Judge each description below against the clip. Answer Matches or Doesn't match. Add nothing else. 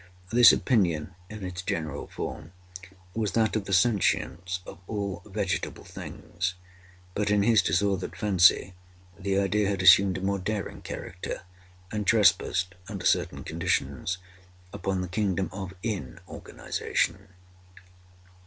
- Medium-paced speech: Doesn't match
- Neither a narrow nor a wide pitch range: Doesn't match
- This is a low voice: Matches